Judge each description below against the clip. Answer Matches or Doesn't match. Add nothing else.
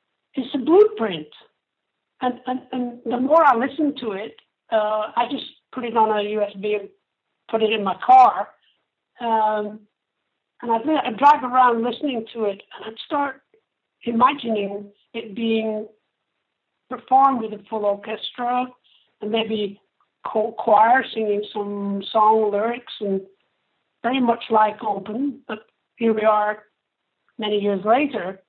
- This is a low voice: Doesn't match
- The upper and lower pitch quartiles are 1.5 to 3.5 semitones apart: Matches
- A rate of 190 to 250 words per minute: Doesn't match